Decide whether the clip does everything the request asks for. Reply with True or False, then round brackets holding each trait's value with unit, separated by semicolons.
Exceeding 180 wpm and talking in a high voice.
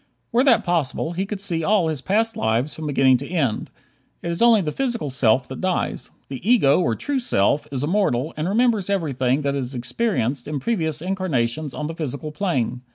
False (200 wpm; 155 Hz)